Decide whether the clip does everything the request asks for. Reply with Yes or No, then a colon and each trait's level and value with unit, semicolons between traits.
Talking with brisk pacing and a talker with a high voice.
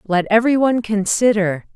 No: slow, 105 wpm; high, 210 Hz